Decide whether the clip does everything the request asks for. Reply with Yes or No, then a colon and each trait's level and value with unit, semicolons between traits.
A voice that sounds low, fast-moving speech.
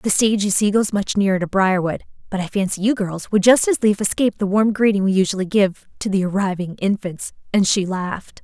No: high, 200 Hz; fast, 230 wpm